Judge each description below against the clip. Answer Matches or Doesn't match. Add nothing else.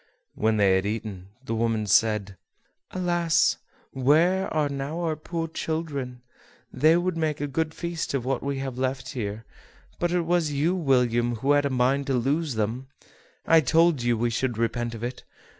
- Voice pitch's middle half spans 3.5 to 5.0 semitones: Doesn't match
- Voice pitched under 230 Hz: Matches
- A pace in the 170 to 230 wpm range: Matches